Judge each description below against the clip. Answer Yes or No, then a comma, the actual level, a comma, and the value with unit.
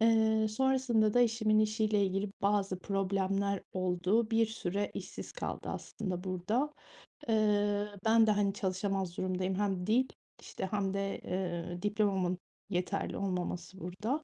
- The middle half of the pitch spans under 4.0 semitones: Yes, average, 2.7 semitones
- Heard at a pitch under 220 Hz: Yes, high, 200 Hz